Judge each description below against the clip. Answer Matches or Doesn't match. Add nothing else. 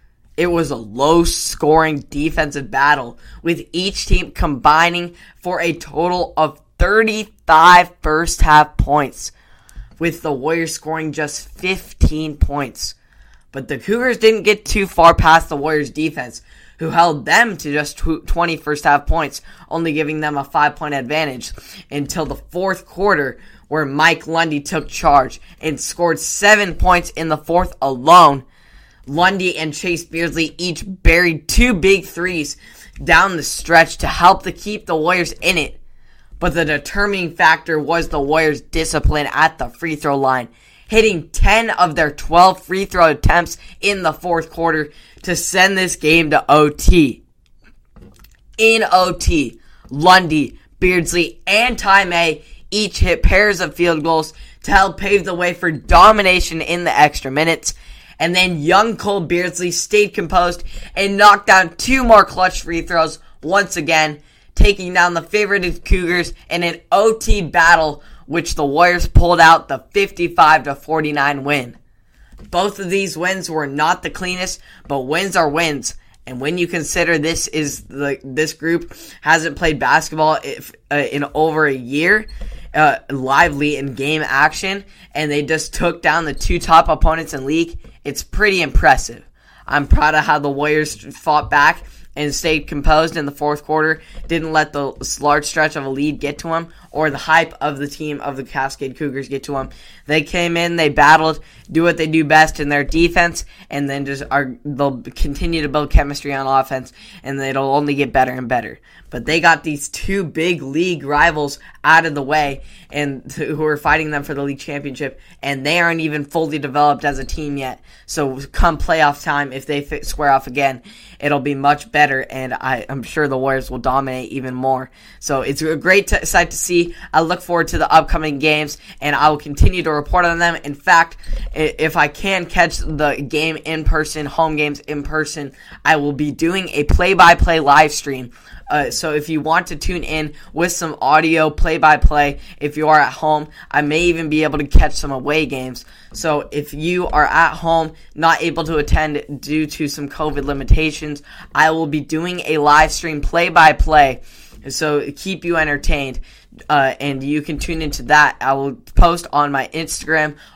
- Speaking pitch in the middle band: Matches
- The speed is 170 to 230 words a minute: Matches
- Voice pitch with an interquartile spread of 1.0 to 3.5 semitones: Matches